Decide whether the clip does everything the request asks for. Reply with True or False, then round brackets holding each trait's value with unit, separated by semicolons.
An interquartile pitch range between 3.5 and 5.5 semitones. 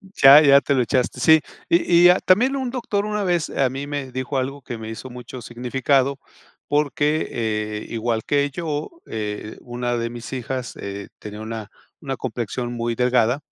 True (3.8 semitones)